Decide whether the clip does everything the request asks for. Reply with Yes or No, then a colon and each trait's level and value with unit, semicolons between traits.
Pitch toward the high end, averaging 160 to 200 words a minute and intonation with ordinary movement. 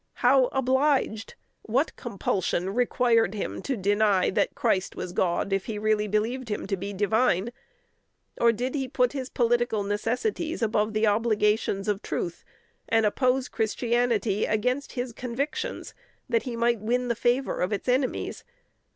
No: high, 230 Hz; average, 150 wpm; average, 3.3 semitones